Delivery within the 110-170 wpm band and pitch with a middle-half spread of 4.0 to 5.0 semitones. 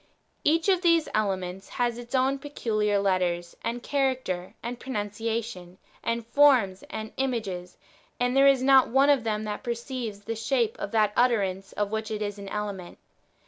Yes: average, 165 wpm; average, 4.3 semitones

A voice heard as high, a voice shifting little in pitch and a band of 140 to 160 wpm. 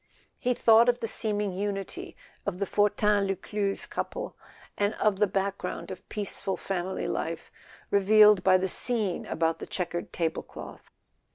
Yes: high, 200 Hz; narrow, 2.0 semitones; average, 155 wpm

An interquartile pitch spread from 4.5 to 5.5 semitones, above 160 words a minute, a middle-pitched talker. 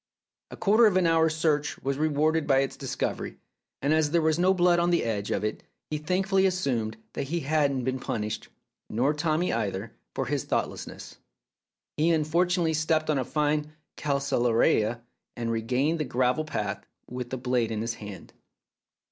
Yes: average, 4.9 semitones; average, 175 wpm; medium, 150 Hz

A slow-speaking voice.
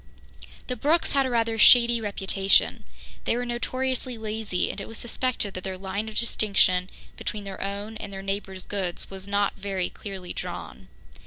No: average, 170 wpm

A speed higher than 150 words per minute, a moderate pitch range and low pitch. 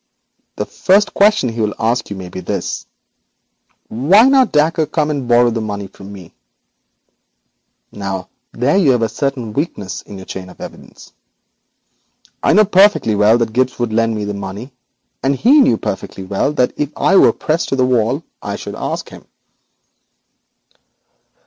No: average, 170 wpm; wide, 6.5 semitones; low, 120 Hz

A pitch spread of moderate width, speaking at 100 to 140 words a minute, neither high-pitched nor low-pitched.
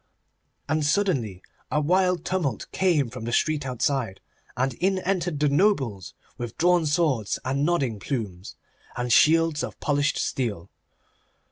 No: wide, 6.2 semitones; slow, 135 wpm; medium, 145 Hz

